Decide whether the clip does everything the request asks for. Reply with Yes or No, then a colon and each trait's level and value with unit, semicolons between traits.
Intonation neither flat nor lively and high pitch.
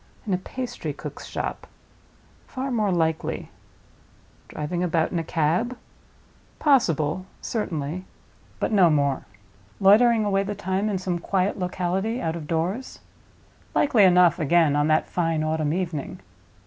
No: average, 4.2 semitones; medium, 180 Hz